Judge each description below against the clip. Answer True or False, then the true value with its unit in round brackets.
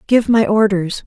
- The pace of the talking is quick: False (170 wpm)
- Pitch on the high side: True (210 Hz)